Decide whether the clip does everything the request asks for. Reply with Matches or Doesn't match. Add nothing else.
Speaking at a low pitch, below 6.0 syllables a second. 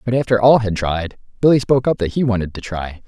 Doesn't match